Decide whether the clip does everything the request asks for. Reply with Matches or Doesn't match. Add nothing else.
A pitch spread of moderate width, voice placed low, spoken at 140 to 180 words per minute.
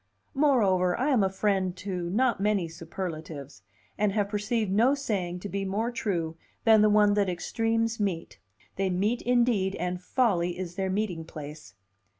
Doesn't match